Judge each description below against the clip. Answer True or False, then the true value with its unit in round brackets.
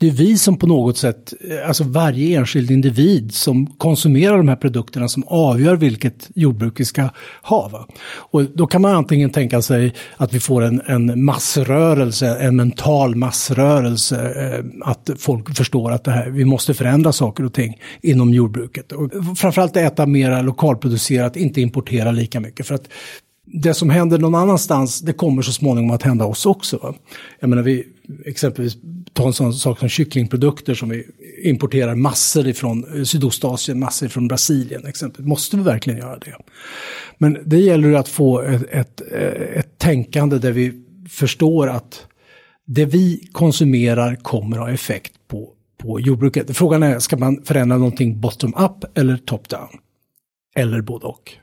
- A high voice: False (135 Hz)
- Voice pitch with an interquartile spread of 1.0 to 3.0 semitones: False (3.5 semitones)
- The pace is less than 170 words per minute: True (160 wpm)